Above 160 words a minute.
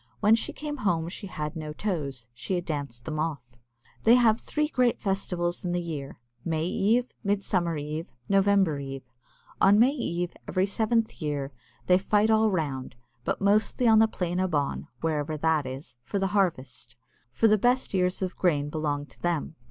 Yes: average, 180 wpm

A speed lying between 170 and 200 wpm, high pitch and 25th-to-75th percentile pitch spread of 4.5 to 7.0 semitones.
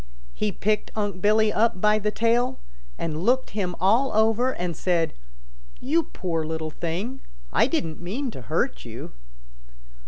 No: average, 150 wpm; high, 210 Hz; average, 5.0 semitones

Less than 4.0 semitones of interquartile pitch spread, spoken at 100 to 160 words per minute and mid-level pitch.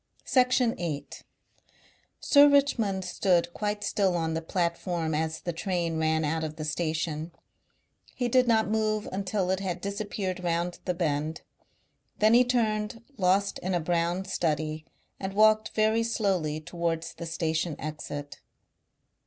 No: average, 4.7 semitones; average, 140 wpm; medium, 180 Hz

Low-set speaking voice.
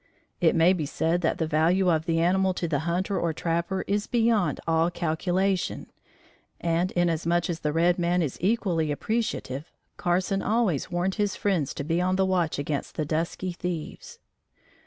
No: medium, 175 Hz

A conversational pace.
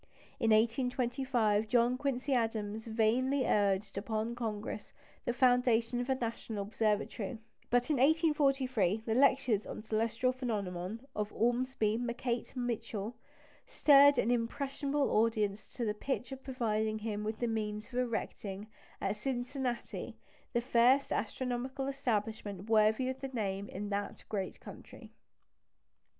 No: slow, 125 wpm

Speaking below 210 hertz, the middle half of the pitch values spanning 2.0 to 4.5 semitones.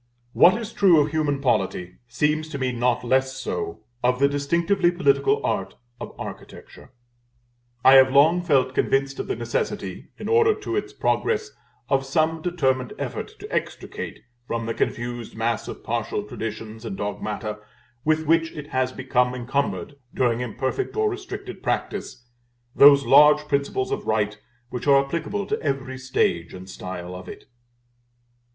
No: low, 135 Hz; average, 5.2 semitones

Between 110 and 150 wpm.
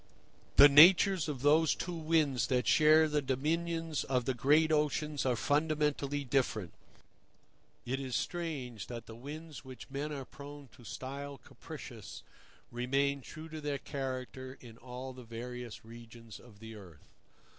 Yes: average, 145 wpm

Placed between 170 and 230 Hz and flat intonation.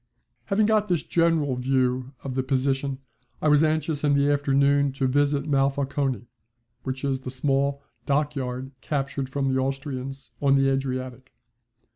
No: low, 135 Hz; narrow, 1.5 semitones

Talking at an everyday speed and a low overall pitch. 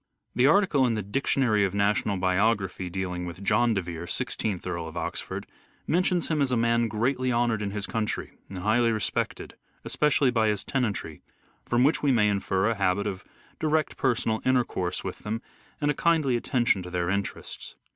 Yes: average, 180 wpm; low, 110 Hz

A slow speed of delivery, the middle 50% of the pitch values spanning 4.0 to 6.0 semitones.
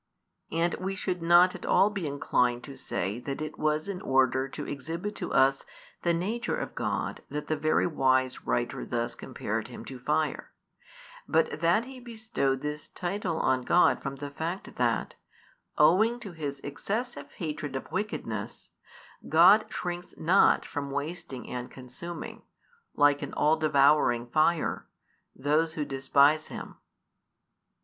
No: average, 145 wpm; average, 4.5 semitones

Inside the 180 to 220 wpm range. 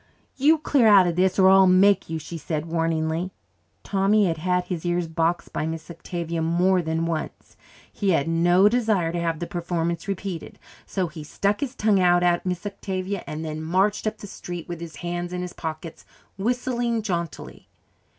Yes: average, 185 wpm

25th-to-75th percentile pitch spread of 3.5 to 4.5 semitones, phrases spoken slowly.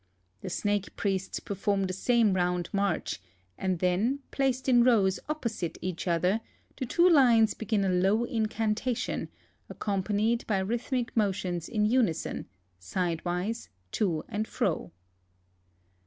Yes: average, 4.0 semitones; slow, 125 wpm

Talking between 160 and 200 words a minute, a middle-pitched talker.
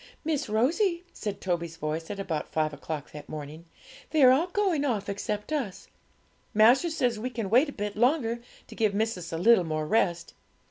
No: average, 185 wpm; high, 215 Hz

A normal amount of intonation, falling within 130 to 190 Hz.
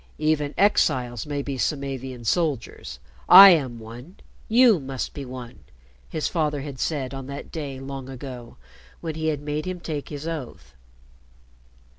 Yes: average, 3.3 semitones; medium, 140 Hz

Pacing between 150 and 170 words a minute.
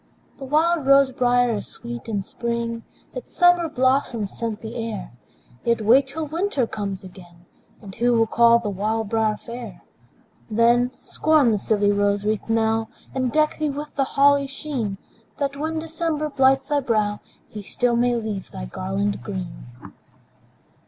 Yes: average, 160 wpm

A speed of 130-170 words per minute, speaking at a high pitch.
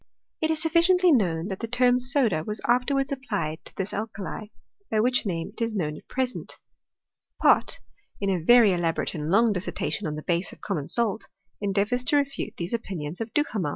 No: average, 190 wpm; high, 215 Hz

